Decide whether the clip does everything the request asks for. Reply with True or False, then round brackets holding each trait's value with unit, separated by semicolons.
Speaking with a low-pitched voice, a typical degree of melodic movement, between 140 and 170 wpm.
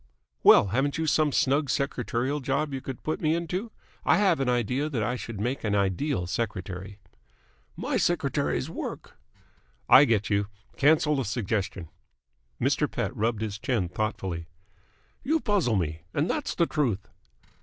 False (125 Hz; 6.5 semitones; 155 wpm)